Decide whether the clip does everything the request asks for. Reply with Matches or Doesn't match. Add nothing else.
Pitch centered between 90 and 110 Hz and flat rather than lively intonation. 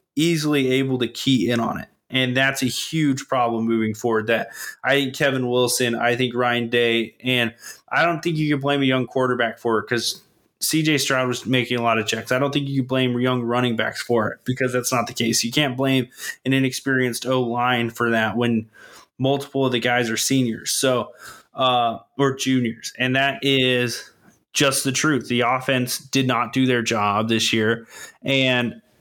Doesn't match